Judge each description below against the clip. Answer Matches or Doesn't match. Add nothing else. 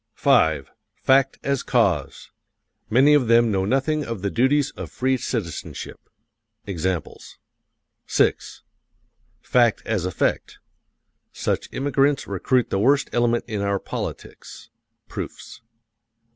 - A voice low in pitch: Matches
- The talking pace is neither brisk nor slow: Doesn't match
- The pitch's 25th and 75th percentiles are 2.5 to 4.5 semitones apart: Doesn't match